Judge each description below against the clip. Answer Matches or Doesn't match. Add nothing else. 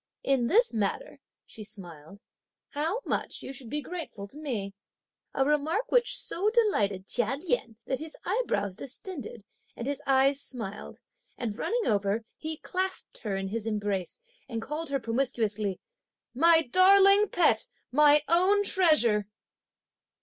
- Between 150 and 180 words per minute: Doesn't match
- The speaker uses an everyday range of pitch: Doesn't match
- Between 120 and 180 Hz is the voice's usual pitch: Doesn't match